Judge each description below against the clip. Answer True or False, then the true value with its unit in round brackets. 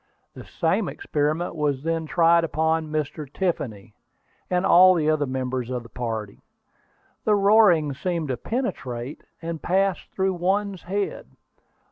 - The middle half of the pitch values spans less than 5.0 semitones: False (5.3 semitones)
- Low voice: False (160 Hz)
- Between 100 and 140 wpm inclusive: True (135 wpm)